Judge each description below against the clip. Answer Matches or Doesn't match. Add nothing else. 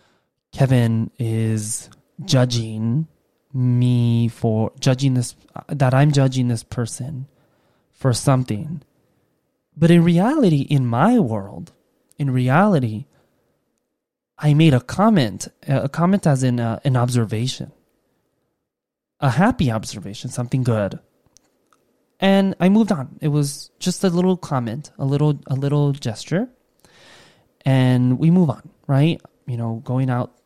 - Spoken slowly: Matches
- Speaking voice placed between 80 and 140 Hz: Matches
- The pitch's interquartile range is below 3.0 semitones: Doesn't match